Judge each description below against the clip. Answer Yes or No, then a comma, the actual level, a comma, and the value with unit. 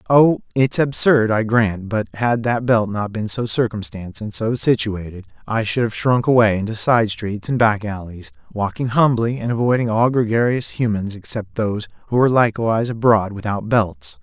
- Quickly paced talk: No, average, 175 wpm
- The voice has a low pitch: Yes, low, 110 Hz